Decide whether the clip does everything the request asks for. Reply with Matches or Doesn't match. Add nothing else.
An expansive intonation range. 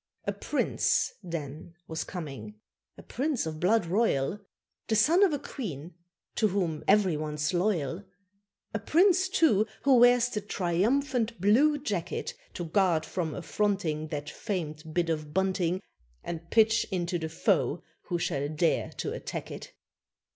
Matches